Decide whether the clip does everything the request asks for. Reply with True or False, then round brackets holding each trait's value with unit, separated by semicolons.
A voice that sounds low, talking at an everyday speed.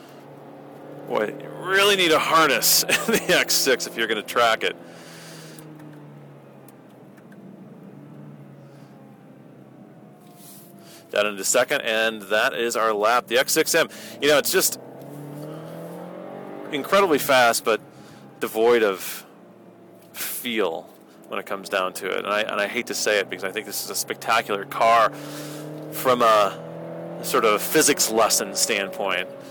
False (115 Hz; 130 wpm)